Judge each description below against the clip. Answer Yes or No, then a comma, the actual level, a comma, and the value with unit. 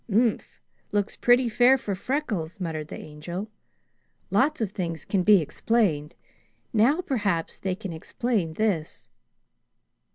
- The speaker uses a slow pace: Yes, slow, 125 wpm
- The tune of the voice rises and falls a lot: Yes, wide, 6.0 semitones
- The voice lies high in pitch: Yes, high, 200 Hz